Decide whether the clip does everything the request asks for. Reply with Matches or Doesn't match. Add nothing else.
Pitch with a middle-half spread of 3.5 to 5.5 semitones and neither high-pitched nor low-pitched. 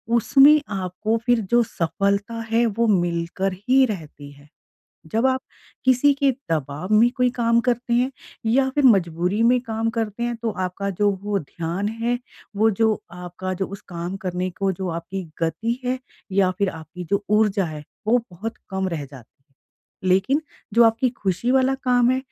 Doesn't match